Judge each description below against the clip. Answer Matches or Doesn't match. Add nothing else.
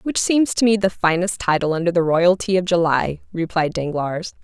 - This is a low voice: Doesn't match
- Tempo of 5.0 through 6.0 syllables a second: Matches